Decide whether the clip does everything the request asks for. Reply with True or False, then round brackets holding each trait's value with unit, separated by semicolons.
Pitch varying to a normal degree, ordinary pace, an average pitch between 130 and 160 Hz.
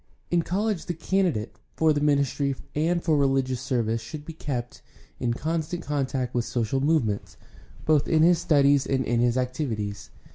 True (4.6 semitones; 170 wpm; 140 Hz)